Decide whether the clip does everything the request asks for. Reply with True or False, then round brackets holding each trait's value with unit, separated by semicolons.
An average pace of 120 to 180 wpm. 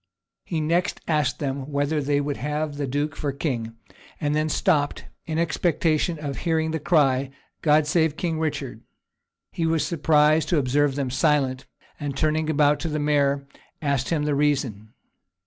True (165 wpm)